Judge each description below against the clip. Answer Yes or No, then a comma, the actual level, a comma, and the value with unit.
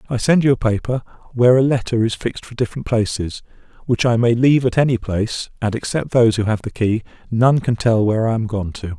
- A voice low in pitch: Yes, low, 115 Hz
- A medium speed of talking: No, fast, 235 wpm